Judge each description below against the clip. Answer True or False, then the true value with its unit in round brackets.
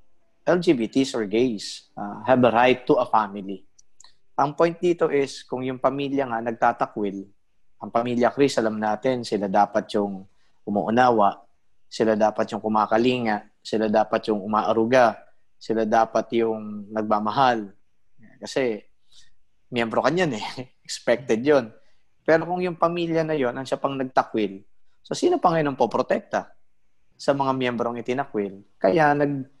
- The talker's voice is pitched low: True (115 Hz)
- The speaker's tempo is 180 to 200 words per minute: False (140 wpm)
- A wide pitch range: False (4.1 semitones)